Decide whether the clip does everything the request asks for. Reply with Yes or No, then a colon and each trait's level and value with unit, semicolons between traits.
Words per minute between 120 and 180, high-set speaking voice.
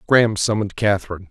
No: average, 140 wpm; low, 100 Hz